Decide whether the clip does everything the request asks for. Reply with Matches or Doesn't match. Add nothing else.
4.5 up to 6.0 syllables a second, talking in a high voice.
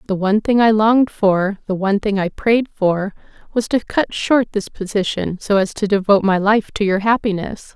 Matches